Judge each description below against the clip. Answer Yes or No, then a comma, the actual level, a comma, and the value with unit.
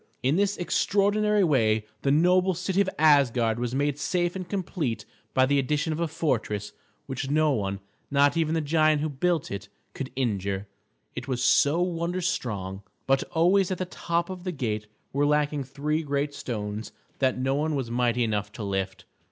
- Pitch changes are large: Yes, wide, 5.9 semitones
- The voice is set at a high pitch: No, medium, 145 Hz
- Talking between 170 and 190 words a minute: Yes, average, 180 wpm